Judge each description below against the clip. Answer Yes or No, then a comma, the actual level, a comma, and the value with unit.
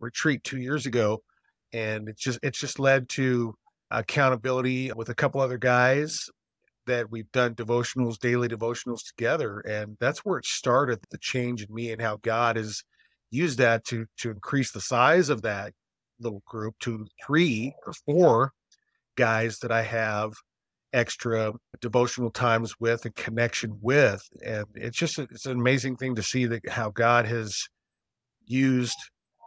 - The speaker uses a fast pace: No, average, 160 wpm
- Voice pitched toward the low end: Yes, low, 120 Hz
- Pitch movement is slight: Yes, narrow, 2.1 semitones